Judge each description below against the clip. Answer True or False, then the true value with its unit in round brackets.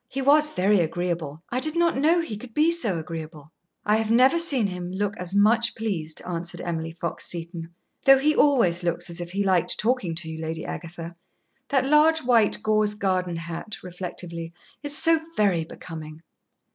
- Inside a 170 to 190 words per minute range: True (180 wpm)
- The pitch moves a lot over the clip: True (7.0 semitones)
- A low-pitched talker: False (190 Hz)